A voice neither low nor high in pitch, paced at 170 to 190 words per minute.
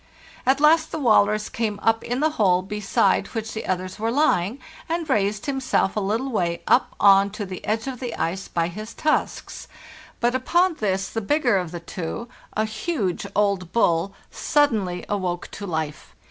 No: high, 210 Hz; average, 185 wpm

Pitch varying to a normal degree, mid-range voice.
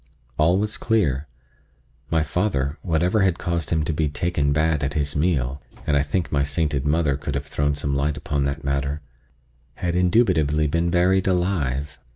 No: average, 3.5 semitones; very low, 75 Hz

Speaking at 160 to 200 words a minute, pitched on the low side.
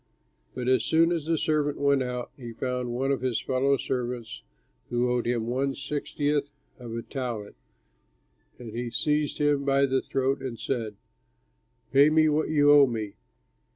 Yes: average, 165 wpm; low, 130 Hz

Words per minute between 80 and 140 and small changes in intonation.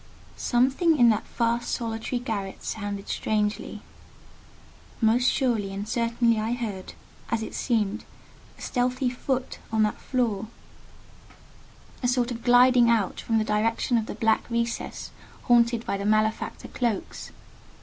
Yes: slow, 135 wpm; narrow, 2.2 semitones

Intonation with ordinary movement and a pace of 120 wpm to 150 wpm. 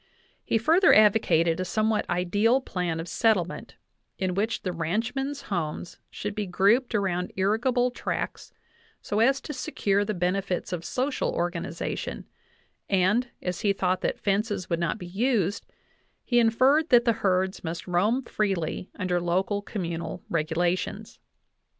Yes: average, 4.1 semitones; average, 145 wpm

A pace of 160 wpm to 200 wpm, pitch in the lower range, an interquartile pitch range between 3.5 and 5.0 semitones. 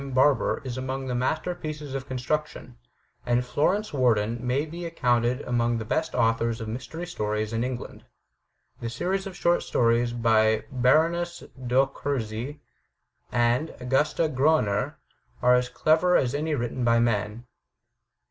No: average, 145 wpm; low, 125 Hz; average, 4.4 semitones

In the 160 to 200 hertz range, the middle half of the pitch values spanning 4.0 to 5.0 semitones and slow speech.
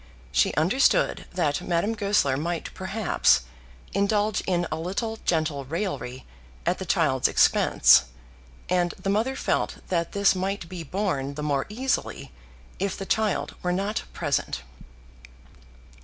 Yes: medium, 185 Hz; average, 4.7 semitones; slow, 130 wpm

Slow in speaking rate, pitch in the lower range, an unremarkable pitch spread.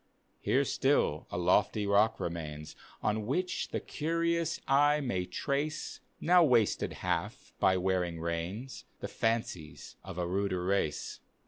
No: slow, 130 wpm; low, 100 Hz; wide, 7.6 semitones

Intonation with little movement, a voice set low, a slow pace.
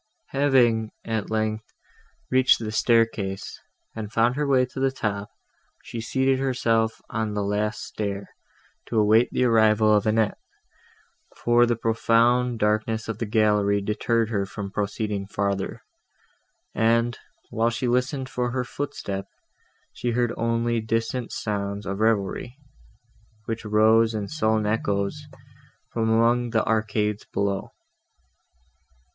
Yes: narrow, 2.1 semitones; low, 110 Hz; slow, 130 wpm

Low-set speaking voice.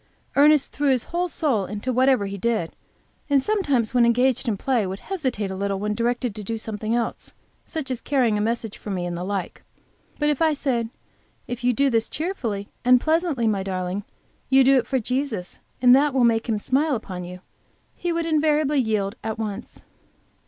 No: high, 240 Hz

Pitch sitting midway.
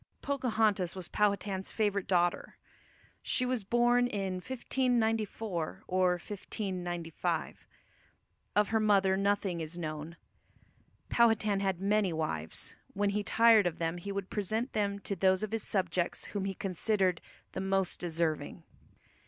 No: high, 195 Hz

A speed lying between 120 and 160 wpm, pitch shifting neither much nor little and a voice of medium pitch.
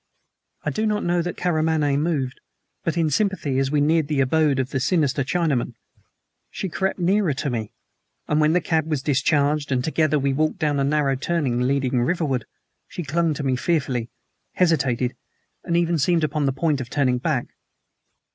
No: average, 180 wpm; average, 3.7 semitones; medium, 150 Hz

